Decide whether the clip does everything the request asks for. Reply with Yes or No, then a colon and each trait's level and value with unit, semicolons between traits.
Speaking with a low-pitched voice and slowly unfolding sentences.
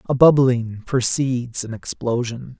Yes: low, 125 Hz; slow, 115 wpm